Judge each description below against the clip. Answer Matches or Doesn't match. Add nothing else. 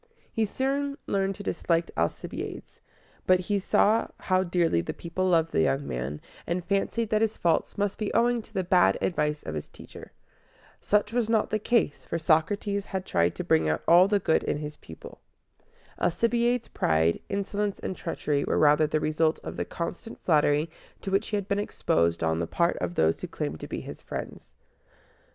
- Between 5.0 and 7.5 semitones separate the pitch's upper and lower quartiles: Matches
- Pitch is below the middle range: Doesn't match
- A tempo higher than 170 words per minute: Matches